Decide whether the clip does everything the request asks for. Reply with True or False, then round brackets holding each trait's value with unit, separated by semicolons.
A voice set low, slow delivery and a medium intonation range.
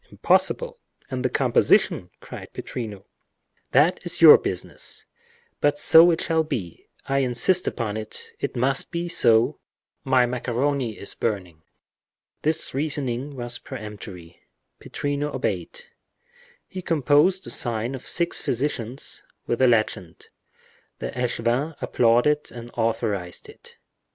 True (125 Hz; 110 wpm; 4.4 semitones)